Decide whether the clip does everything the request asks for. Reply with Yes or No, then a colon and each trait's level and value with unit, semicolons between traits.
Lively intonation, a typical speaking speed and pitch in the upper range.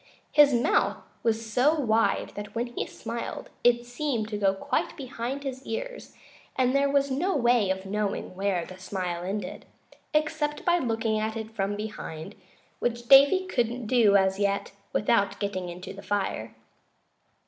No: average, 4.7 semitones; average, 160 wpm; high, 225 Hz